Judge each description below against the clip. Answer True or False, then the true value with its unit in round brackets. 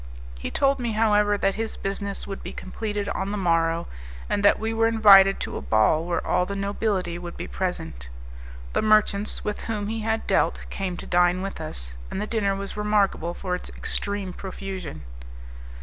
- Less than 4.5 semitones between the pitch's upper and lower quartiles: True (2.8 semitones)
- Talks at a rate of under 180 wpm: False (185 wpm)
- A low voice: False (200 Hz)